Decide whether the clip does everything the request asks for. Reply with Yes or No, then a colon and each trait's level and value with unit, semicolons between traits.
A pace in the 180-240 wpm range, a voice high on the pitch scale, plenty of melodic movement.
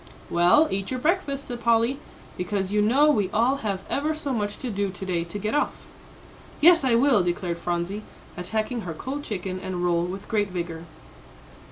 Yes: average, 185 wpm; high, 210 Hz; wide, 6.1 semitones